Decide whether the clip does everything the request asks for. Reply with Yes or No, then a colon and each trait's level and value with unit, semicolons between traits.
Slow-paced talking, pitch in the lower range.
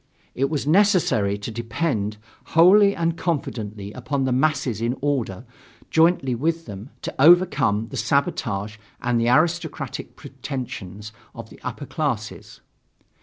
Yes: slow, 125 wpm; low, 130 Hz